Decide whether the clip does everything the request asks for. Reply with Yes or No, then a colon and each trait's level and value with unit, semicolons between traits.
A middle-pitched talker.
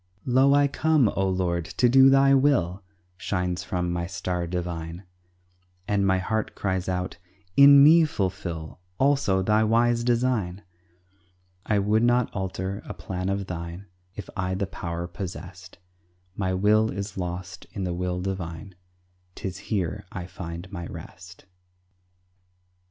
No: very low, 95 Hz